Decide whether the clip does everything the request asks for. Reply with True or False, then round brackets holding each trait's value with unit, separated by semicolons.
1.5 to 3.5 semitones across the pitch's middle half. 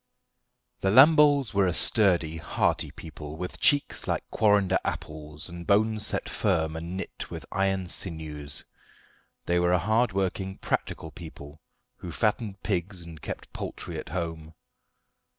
False (4.0 semitones)